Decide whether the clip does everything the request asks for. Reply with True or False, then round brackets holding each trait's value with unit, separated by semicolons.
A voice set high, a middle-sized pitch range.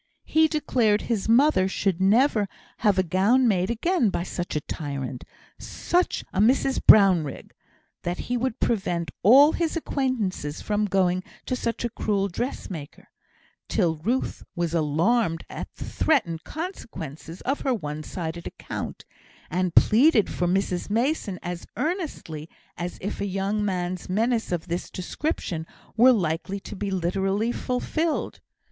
False (195 Hz; 5.7 semitones)